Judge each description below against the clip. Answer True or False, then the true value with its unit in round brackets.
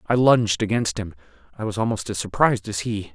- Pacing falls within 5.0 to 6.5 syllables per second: True (6.0 syllables/s)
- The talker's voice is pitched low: True (110 Hz)